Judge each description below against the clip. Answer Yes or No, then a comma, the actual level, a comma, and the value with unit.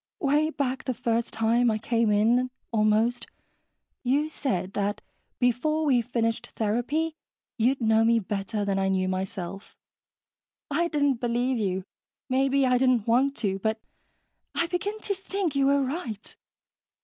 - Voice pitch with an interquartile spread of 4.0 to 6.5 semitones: Yes, average, 4.3 semitones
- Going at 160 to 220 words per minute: No, average, 145 wpm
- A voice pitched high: Yes, high, 240 Hz